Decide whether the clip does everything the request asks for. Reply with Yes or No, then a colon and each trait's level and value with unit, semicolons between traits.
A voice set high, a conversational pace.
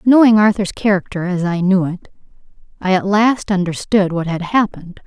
Yes: high, 195 Hz; average, 165 wpm